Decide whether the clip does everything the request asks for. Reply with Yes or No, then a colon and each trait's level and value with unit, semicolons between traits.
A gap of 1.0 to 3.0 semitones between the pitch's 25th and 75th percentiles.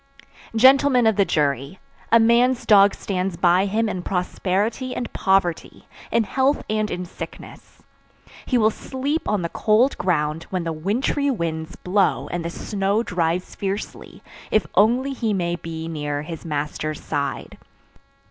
No: average, 5.2 semitones